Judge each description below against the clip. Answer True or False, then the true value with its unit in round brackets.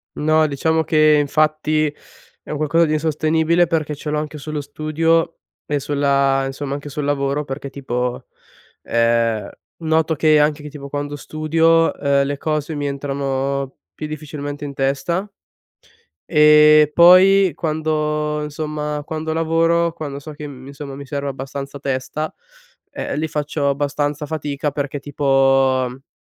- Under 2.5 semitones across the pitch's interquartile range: True (1.9 semitones)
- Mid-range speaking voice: True (150 Hz)